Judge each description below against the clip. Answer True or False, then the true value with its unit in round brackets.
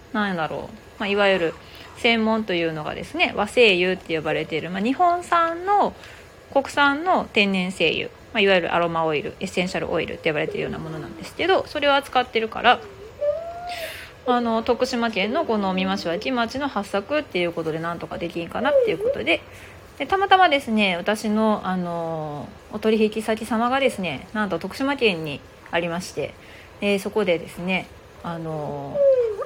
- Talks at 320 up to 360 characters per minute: True (355 characters per minute)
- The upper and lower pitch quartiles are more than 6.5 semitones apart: True (8.0 semitones)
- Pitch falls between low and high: False (215 Hz)